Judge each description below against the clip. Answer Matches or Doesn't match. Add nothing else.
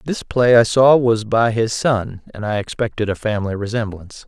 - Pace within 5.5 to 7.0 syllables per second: Doesn't match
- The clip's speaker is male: Matches